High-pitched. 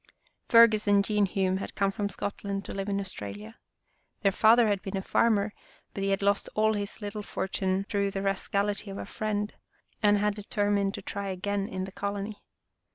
Yes: high, 200 Hz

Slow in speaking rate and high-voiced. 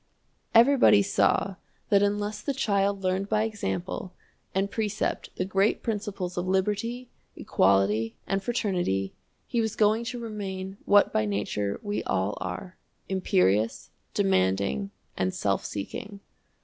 Yes: slow, 125 wpm; high, 195 Hz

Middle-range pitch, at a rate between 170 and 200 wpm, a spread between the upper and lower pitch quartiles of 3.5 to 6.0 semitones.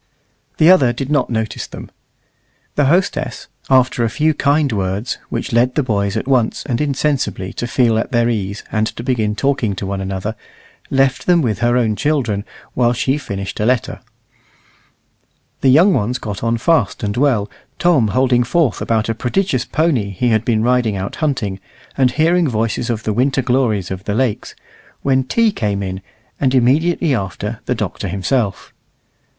No: low, 120 Hz; average, 175 wpm; average, 4.4 semitones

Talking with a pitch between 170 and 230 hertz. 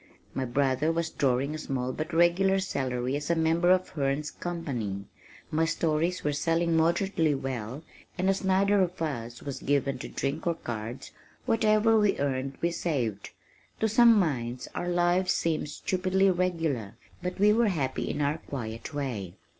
No: medium, 160 Hz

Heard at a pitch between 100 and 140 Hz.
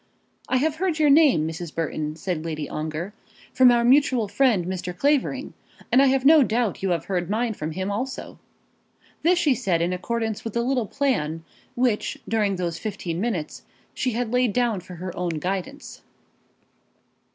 No: high, 215 Hz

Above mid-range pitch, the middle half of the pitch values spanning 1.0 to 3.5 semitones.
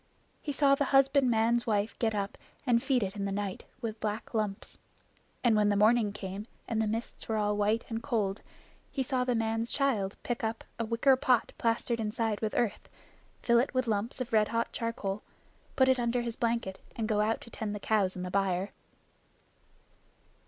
Yes: high, 225 Hz; narrow, 2.4 semitones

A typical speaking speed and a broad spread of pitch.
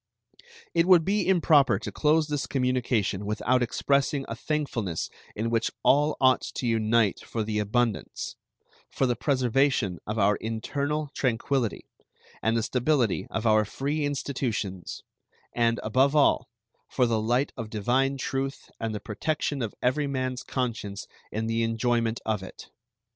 No: average, 145 wpm; average, 3.9 semitones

